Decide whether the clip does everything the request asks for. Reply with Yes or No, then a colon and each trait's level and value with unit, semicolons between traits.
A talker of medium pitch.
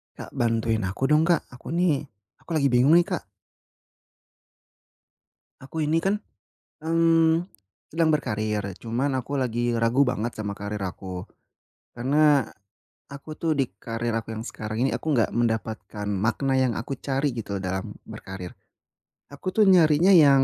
No: low, 130 Hz